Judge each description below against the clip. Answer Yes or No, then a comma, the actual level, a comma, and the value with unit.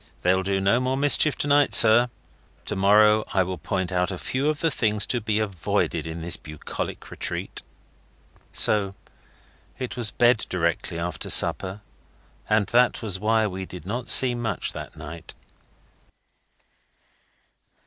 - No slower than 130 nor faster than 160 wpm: Yes, average, 150 wpm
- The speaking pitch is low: Yes, low, 105 Hz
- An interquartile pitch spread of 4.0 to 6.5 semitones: Yes, average, 4.5 semitones